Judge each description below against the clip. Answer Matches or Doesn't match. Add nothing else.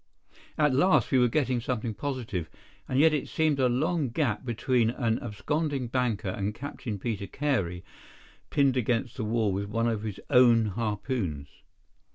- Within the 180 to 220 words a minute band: Doesn't match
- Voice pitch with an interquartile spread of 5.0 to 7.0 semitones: Doesn't match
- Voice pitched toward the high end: Doesn't match